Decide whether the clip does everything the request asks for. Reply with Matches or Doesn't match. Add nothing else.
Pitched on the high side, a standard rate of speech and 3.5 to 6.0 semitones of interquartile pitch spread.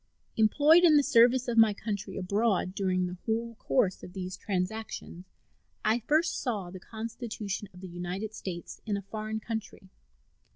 Matches